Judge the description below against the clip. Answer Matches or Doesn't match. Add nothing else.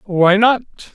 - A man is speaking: Matches